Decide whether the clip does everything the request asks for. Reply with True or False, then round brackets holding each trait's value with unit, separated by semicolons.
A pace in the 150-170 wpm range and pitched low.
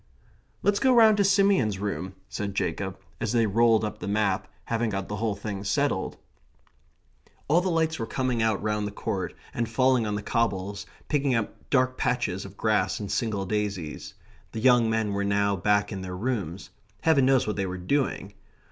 False (185 wpm; 105 Hz)